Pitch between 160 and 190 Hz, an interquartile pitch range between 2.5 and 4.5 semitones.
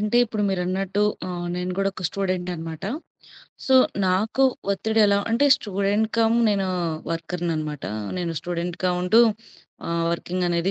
Yes: medium, 185 Hz; average, 2.8 semitones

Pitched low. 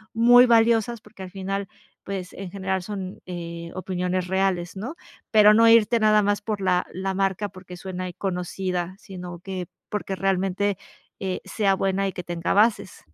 No: high, 195 Hz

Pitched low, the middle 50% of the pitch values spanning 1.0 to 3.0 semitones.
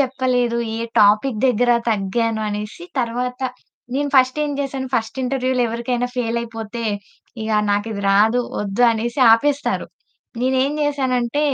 No: high, 245 Hz; narrow, 2.6 semitones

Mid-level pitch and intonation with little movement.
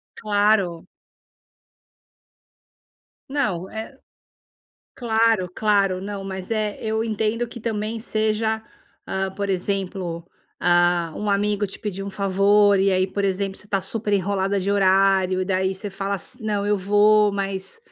No: high, 200 Hz; narrow, 2.0 semitones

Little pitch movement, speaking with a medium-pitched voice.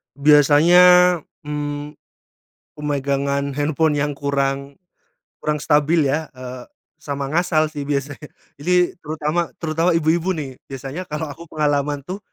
Yes: narrow, 2.3 semitones; medium, 150 Hz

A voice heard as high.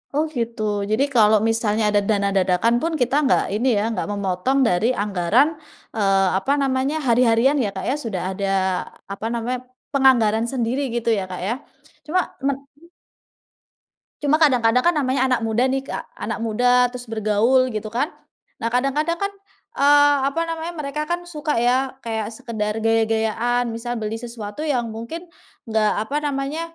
Yes: high, 240 Hz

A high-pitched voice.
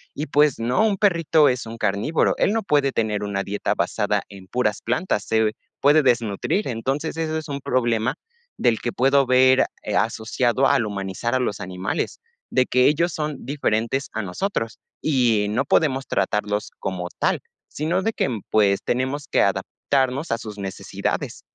No: low, 125 Hz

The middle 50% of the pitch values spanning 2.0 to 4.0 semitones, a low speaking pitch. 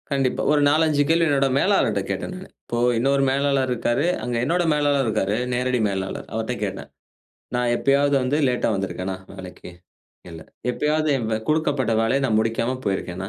No: average, 4.8 semitones; low, 130 Hz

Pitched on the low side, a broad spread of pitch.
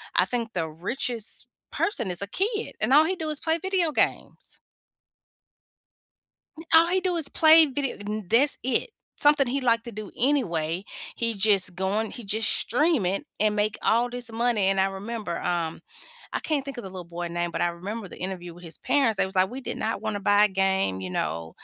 No: high, 215 Hz; wide, 6.2 semitones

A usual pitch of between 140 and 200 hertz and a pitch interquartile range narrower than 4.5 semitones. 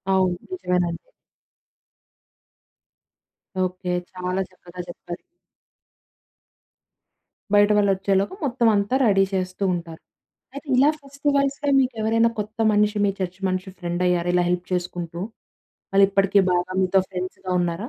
Yes: high, 190 Hz; average, 2.9 semitones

